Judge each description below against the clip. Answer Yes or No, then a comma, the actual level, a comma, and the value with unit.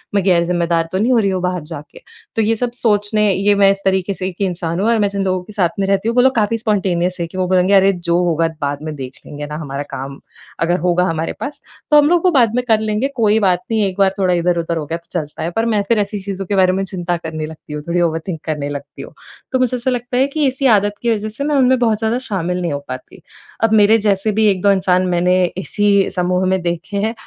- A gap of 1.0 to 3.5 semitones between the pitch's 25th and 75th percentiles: No, average, 3.9 semitones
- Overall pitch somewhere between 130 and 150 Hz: No, high, 190 Hz